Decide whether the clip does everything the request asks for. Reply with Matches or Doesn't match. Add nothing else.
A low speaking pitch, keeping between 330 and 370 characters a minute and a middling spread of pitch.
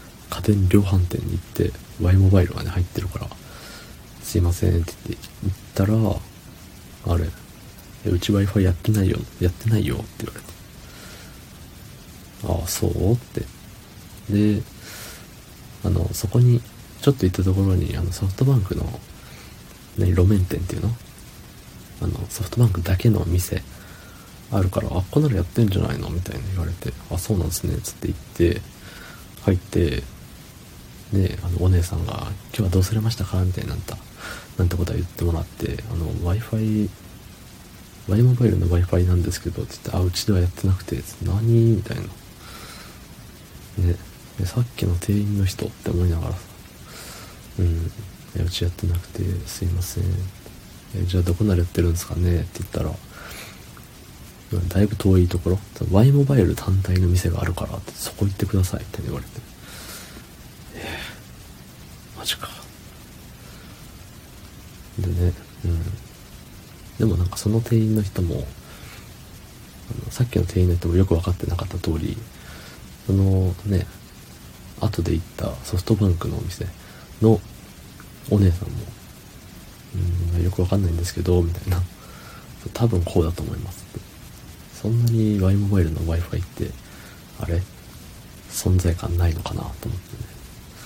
Doesn't match